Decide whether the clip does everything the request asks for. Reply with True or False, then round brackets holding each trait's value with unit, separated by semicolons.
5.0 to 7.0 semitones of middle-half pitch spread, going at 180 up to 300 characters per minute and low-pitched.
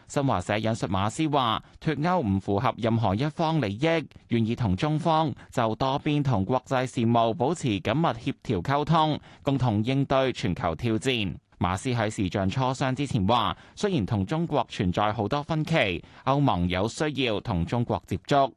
True (5.6 semitones; 255 characters per minute; 130 Hz)